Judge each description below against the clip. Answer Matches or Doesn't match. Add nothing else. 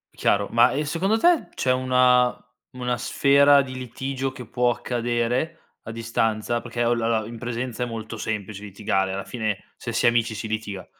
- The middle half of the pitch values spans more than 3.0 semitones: Doesn't match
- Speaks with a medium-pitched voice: Doesn't match